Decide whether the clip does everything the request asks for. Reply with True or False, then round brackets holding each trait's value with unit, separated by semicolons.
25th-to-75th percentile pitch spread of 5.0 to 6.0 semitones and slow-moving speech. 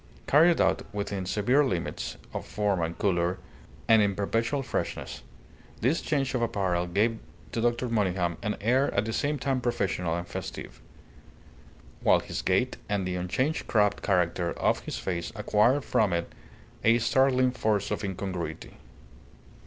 False (5.3 semitones; 150 wpm)